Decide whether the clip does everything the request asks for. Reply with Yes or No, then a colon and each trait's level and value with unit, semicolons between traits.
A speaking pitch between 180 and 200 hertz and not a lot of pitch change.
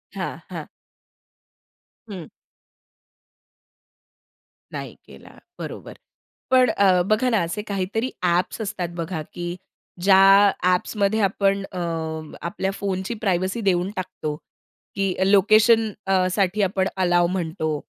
Yes: high, 190 Hz; narrow, 2.2 semitones